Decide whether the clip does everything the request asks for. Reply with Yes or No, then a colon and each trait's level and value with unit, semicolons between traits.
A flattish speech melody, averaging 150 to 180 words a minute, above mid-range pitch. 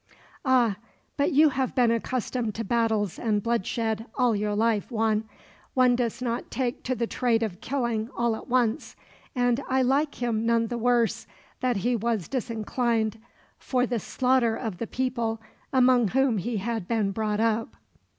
Yes: narrow, 2.1 semitones; average, 165 wpm; high, 235 Hz